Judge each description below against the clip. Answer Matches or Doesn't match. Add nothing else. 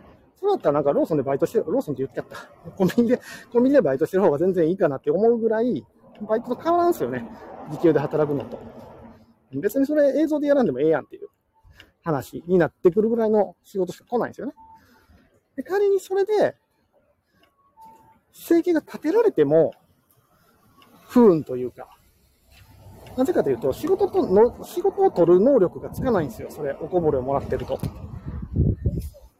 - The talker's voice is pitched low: Doesn't match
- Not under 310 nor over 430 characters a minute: Matches